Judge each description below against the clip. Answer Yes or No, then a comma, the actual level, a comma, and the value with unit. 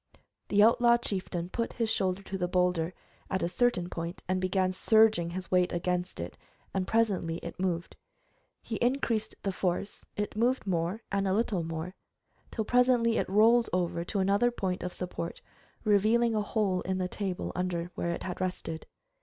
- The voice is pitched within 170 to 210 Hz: Yes, high, 190 Hz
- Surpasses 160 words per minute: Yes, average, 175 wpm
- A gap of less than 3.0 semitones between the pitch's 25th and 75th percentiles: No, average, 3.6 semitones